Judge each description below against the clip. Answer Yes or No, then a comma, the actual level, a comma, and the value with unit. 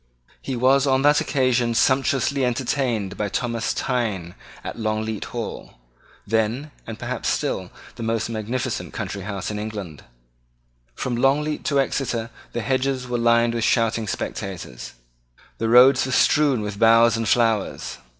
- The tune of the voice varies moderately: Yes, average, 3.1 semitones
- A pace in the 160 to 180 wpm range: No, average, 140 wpm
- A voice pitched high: No, low, 115 Hz